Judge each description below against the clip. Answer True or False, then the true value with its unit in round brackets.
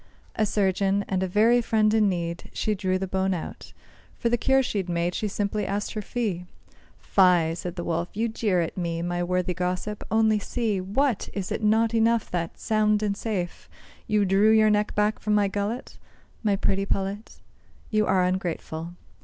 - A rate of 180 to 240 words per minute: True (185 wpm)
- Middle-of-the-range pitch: False (200 Hz)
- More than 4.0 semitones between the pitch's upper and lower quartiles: False (2.9 semitones)